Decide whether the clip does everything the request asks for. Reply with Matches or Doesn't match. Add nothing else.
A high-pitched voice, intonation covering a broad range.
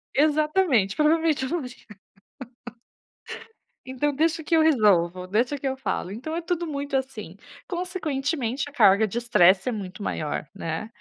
Matches